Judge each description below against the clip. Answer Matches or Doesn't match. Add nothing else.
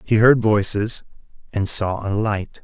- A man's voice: Matches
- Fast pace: Doesn't match